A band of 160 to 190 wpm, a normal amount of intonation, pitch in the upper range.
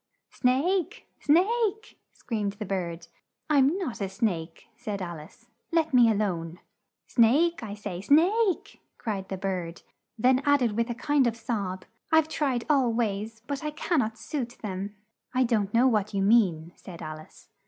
No: average, 170 wpm; wide, 6.5 semitones; high, 230 Hz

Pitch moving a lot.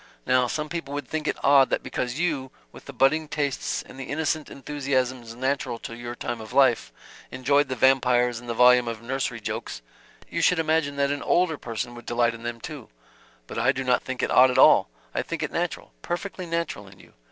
No: average, 3.1 semitones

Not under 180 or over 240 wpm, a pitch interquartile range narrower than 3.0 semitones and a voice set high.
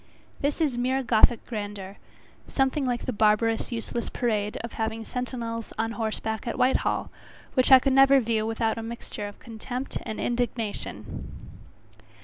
No: average, 145 wpm; narrow, 2.4 semitones; high, 230 Hz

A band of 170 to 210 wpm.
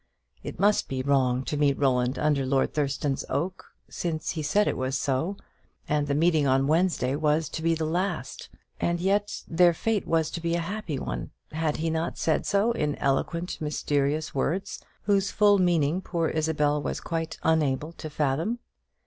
Yes: average, 175 wpm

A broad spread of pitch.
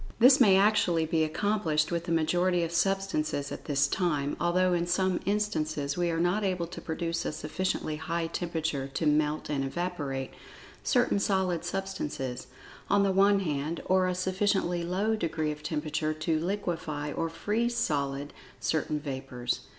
No: average, 3.7 semitones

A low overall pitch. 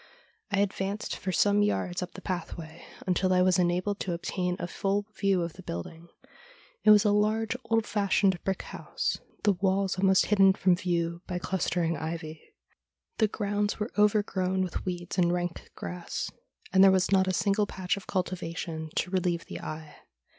No: medium, 185 Hz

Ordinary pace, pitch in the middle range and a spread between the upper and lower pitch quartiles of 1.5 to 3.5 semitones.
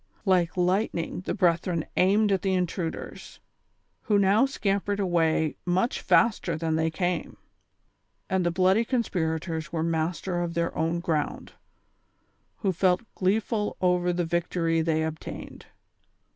No: slow, 130 wpm; medium, 180 Hz; average, 2.8 semitones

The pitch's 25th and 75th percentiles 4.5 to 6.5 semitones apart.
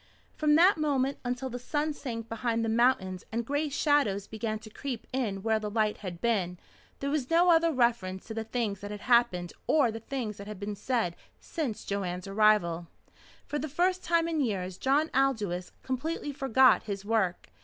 Yes: wide, 5.4 semitones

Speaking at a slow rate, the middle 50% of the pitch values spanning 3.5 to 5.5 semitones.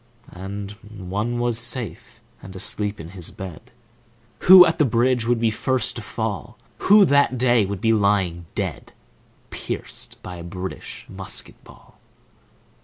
No: average, 145 wpm; average, 4.2 semitones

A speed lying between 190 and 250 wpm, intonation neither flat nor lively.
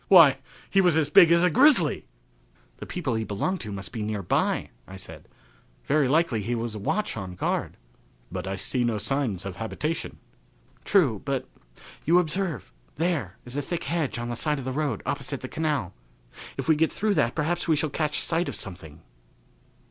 No: average, 195 wpm; wide, 7.1 semitones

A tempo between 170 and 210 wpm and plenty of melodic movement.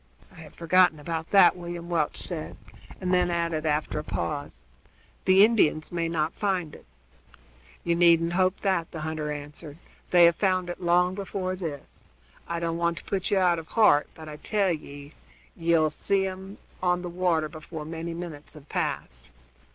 No: average, 175 wpm; average, 2.7 semitones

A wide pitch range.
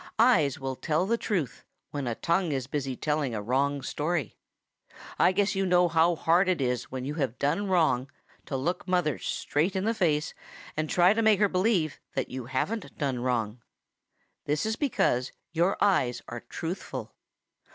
Yes: wide, 5.8 semitones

